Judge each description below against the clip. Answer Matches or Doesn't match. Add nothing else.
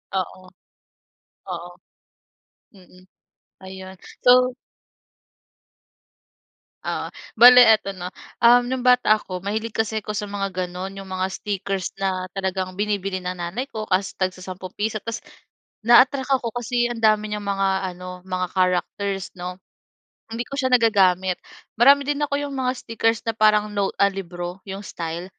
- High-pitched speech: Matches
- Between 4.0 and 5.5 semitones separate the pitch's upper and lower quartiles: Doesn't match